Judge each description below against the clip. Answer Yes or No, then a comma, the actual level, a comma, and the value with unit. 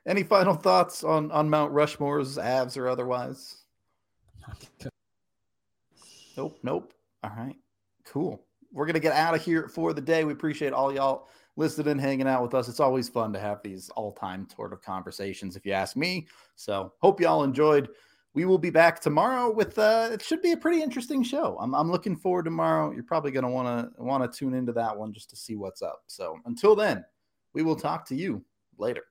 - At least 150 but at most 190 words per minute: No, average, 200 wpm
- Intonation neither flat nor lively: No, wide, 6.4 semitones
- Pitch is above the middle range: No, medium, 145 Hz